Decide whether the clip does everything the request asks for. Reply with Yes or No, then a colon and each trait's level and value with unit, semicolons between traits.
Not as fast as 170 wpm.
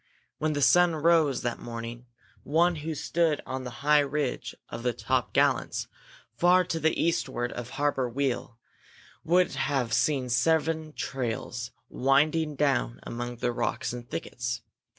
Yes: average, 145 wpm